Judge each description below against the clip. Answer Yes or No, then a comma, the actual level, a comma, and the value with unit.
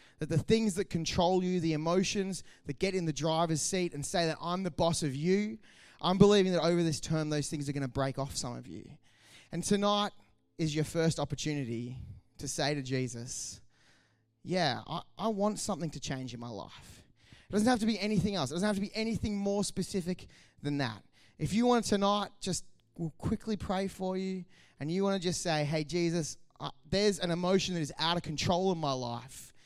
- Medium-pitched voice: Yes, medium, 170 Hz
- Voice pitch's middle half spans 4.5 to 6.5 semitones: Yes, average, 5.0 semitones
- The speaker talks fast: Yes, fast, 210 wpm